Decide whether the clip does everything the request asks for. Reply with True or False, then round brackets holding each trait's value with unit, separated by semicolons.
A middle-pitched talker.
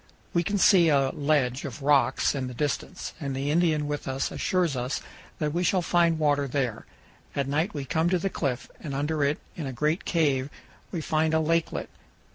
True (150 Hz)